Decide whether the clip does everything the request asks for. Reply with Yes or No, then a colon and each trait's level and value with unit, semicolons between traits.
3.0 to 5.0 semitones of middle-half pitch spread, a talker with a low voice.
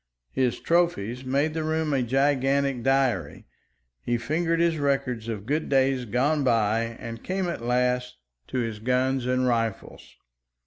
Yes: average, 3.5 semitones; low, 130 Hz